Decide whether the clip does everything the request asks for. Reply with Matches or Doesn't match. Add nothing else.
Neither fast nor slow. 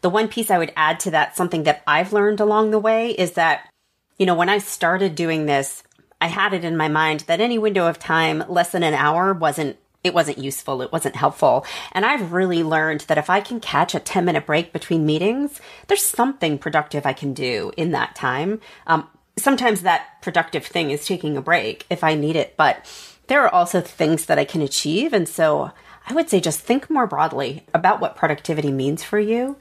Doesn't match